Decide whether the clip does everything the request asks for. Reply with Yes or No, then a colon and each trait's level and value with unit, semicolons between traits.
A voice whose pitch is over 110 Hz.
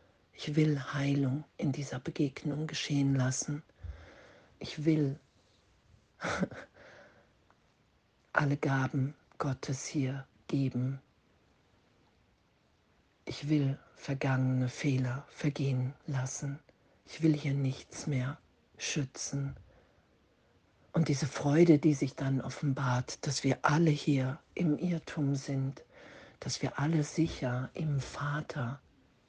Yes: medium, 140 Hz